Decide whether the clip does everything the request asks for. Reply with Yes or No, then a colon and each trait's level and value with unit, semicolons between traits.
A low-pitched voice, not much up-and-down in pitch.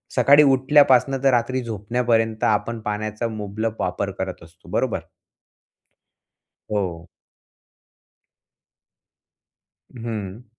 No: low, 110 Hz; average, 3.3 semitones